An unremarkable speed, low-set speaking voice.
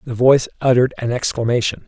Yes: average, 160 wpm; low, 125 Hz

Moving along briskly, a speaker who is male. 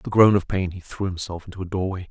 Yes: fast, 315 wpm; male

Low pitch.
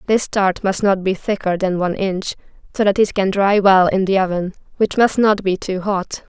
No: high, 195 Hz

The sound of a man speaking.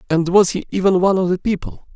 Yes: male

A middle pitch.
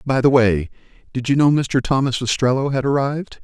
No: low, 130 Hz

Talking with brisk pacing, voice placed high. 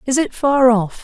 Yes: fast, 235 wpm; very high, 255 Hz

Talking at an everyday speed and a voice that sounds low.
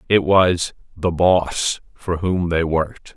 Yes: average, 150 wpm; very low, 85 Hz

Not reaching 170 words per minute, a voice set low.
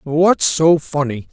No: slow, 135 wpm; medium, 145 Hz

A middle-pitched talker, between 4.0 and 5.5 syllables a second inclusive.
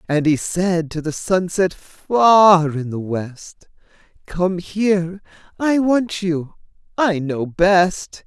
No: medium, 180 Hz; 3.0 syllables/s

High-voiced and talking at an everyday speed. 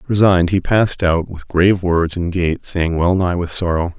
No: very low, 90 Hz; average, 195 wpm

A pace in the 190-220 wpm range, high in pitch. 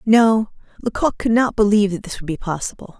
Yes: average, 200 wpm; high, 210 Hz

